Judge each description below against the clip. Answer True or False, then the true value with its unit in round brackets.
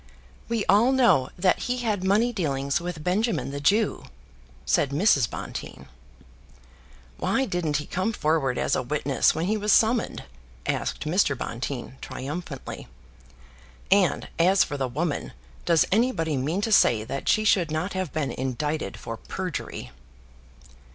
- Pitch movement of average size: False (6.5 semitones)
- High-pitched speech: False (165 Hz)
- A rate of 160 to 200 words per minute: False (145 wpm)